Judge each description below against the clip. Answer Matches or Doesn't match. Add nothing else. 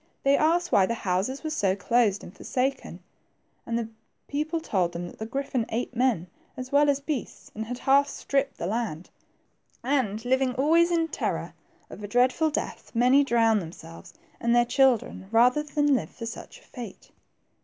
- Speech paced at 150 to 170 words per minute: Doesn't match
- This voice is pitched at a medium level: Doesn't match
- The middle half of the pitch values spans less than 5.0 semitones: Matches